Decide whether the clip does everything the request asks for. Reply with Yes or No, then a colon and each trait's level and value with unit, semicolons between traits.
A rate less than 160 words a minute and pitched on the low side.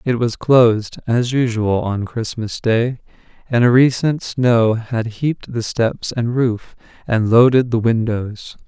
Yes: average, 150 wpm; low, 120 Hz